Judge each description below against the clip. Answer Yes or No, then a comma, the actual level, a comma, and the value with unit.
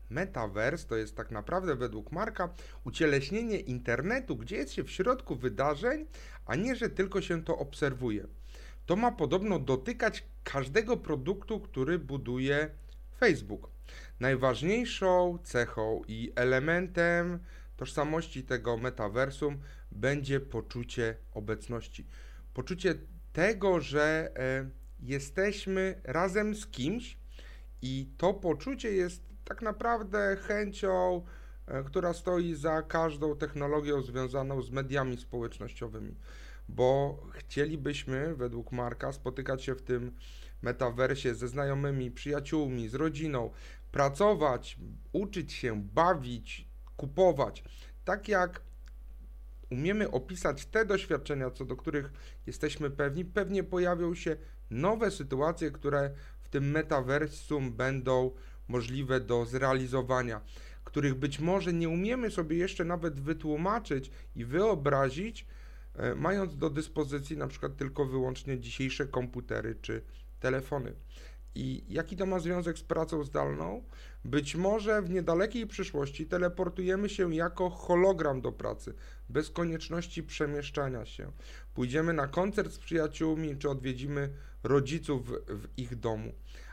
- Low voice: No, medium, 145 Hz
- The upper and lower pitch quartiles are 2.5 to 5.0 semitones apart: No, wide, 5.6 semitones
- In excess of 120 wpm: No, average, 115 wpm